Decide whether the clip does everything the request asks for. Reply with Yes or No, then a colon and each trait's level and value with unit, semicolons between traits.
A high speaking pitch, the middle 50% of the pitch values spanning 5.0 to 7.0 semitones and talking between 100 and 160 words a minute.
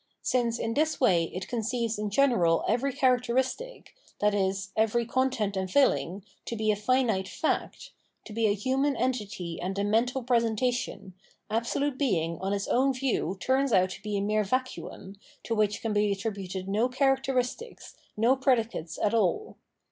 No: high, 225 Hz; average, 4.4 semitones; average, 155 wpm